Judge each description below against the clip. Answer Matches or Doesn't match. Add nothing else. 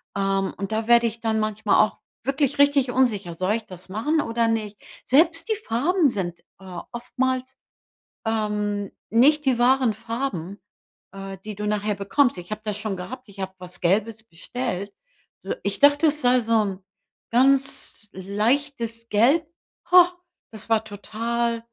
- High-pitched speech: Matches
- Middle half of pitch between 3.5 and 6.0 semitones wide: Matches